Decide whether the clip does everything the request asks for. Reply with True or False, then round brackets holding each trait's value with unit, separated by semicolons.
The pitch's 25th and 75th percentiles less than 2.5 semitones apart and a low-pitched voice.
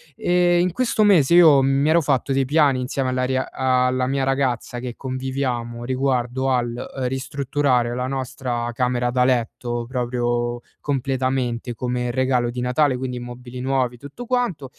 True (1.8 semitones; 130 Hz)